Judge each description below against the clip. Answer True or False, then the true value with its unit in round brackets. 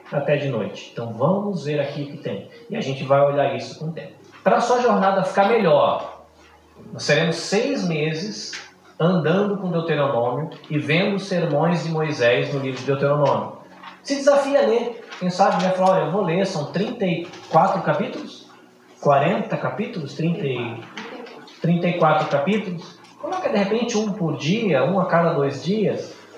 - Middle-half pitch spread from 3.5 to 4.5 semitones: False (5.3 semitones)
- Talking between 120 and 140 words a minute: False (160 wpm)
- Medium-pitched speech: True (170 Hz)